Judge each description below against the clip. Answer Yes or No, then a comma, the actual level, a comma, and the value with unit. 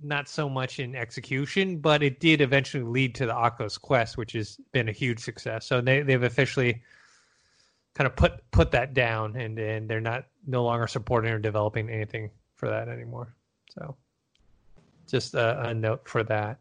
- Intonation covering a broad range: No, average, 3.2 semitones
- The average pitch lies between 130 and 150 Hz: No, low, 120 Hz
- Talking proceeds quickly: No, average, 180 wpm